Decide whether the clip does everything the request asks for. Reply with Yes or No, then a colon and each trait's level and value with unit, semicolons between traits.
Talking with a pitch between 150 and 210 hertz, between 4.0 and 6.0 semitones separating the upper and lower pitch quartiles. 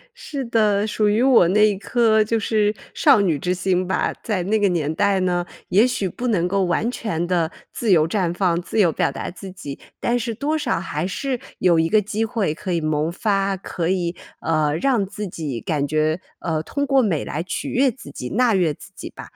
Yes: high, 190 Hz; average, 4.6 semitones